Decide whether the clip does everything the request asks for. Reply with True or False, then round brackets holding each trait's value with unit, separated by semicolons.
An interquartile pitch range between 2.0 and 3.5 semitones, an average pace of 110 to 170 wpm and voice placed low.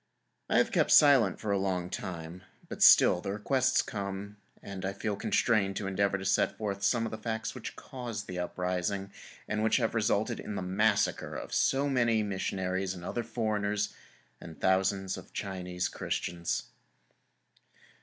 True (2.6 semitones; 160 wpm; 100 Hz)